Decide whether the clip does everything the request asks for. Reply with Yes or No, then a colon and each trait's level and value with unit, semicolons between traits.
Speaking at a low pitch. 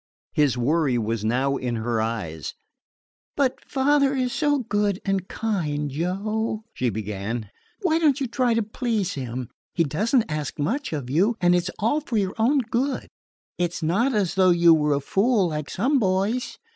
No: medium, 185 Hz